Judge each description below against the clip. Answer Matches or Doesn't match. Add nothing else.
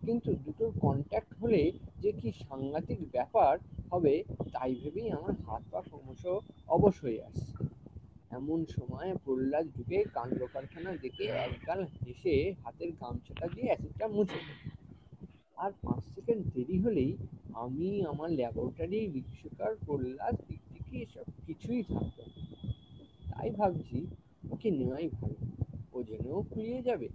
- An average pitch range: Doesn't match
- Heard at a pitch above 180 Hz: Doesn't match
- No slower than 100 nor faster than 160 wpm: Matches